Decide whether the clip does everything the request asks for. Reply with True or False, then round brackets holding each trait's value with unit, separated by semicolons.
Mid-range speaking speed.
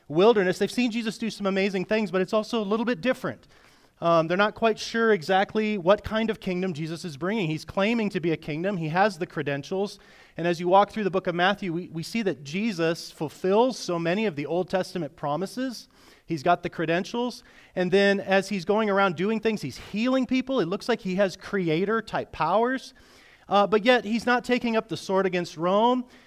False (215 wpm)